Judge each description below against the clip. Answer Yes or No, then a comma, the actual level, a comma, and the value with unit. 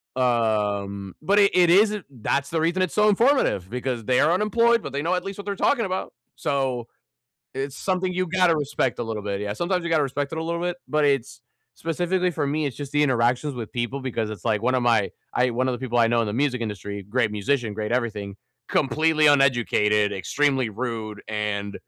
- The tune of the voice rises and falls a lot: Yes, wide, 6.9 semitones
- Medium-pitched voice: No, low, 130 Hz